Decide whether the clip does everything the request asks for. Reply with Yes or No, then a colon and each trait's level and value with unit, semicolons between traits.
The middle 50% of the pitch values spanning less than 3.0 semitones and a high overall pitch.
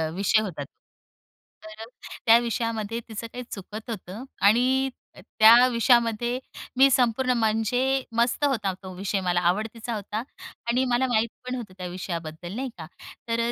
No: average, 3.3 semitones; high, 230 Hz